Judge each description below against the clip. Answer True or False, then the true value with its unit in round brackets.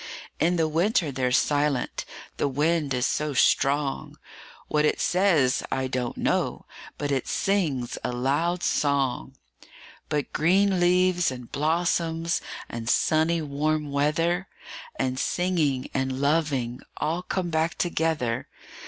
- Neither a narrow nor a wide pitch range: True (4.2 semitones)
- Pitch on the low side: False (150 Hz)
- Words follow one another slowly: True (125 wpm)